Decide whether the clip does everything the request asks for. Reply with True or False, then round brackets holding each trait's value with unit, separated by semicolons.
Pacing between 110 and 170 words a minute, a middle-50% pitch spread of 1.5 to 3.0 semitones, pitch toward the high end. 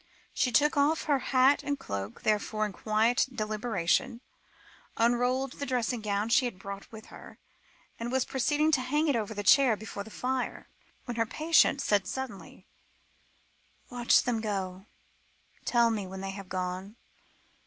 False (155 wpm; 4.4 semitones; 230 Hz)